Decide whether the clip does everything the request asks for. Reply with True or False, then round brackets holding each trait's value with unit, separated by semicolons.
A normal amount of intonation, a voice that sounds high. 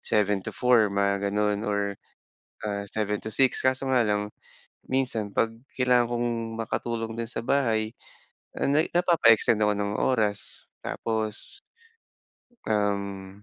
False (3.0 semitones; 110 Hz)